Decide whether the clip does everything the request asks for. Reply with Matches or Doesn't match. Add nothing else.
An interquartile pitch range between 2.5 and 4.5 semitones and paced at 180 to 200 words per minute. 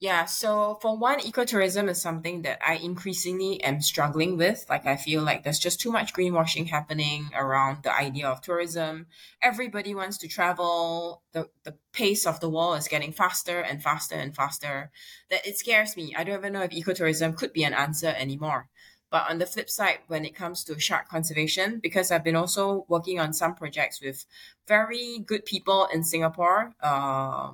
Matches